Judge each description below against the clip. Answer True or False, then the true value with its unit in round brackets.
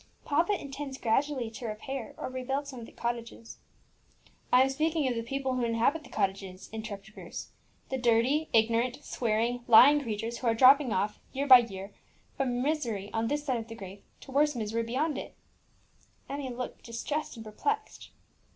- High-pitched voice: True (245 Hz)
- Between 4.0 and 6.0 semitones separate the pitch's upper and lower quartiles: False (3.5 semitones)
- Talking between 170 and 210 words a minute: True (175 wpm)